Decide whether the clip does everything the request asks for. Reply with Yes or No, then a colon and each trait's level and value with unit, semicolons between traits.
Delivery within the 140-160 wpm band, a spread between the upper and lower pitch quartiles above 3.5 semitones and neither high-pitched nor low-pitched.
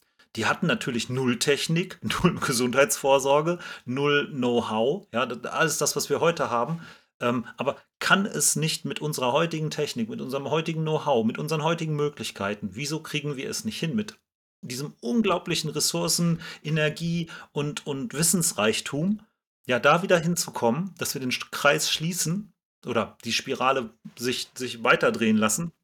Yes: average, 145 wpm; average, 4.7 semitones; medium, 150 Hz